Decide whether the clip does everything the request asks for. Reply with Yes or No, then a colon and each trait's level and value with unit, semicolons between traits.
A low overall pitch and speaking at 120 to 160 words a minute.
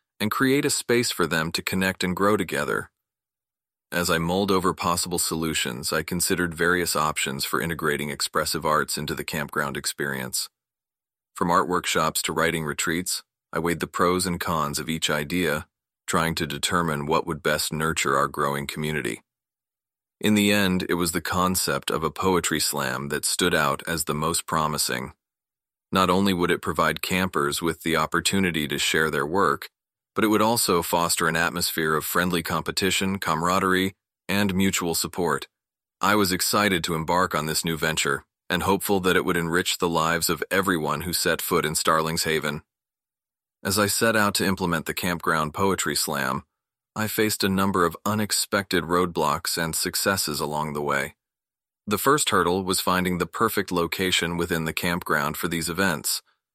No: very low, 85 Hz; average, 170 wpm